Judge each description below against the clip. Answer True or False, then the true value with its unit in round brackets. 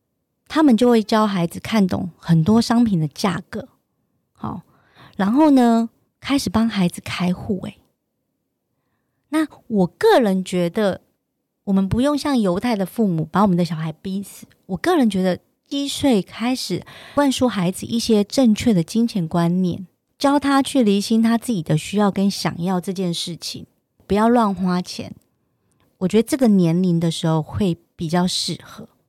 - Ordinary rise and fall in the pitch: True (4.9 semitones)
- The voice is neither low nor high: False (200 Hz)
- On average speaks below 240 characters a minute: True (230 characters per minute)